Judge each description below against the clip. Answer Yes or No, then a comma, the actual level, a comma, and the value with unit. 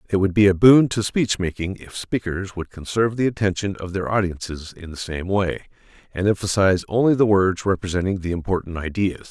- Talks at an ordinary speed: Yes, average, 195 wpm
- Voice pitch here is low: Yes, very low, 95 Hz